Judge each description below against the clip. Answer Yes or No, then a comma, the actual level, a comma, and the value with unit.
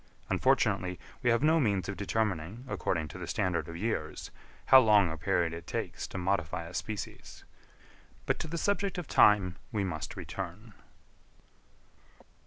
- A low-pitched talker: Yes, very low, 95 Hz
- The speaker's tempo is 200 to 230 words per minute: No, average, 155 wpm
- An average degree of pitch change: Yes, average, 4.8 semitones